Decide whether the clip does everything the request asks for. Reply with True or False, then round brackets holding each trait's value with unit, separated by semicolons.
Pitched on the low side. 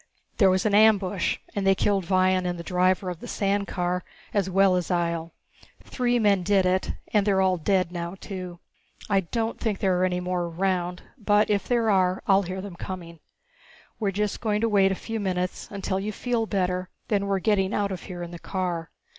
False (190 Hz)